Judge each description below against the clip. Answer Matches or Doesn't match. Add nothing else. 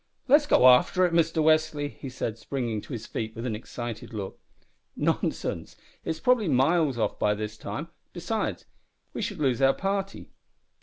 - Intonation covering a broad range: Matches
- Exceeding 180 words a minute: Doesn't match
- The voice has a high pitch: Doesn't match